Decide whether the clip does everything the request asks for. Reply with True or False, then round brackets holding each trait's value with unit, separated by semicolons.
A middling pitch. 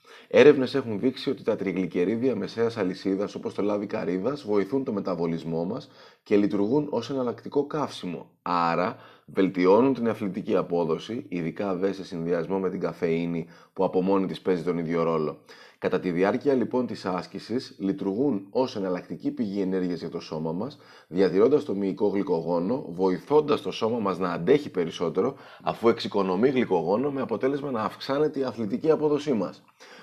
False (100 Hz)